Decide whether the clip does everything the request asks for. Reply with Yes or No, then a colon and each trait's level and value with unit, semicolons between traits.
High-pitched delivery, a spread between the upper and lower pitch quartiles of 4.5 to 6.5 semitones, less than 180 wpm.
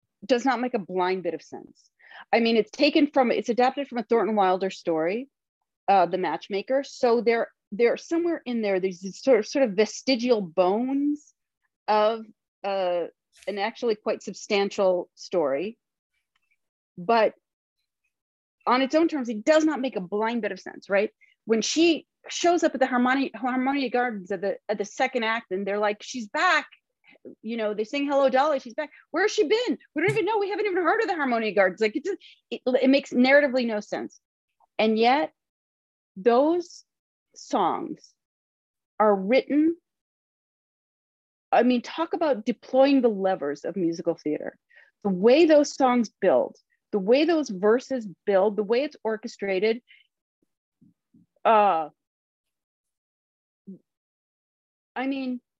Yes: high, 240 Hz; average, 5.3 semitones; average, 155 wpm